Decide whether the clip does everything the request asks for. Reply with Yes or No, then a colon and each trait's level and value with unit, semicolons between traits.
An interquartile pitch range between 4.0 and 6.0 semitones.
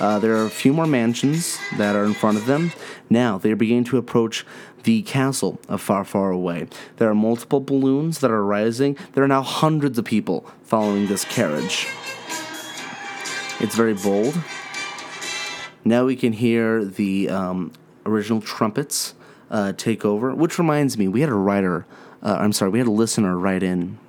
Yes: average, 4.7 semitones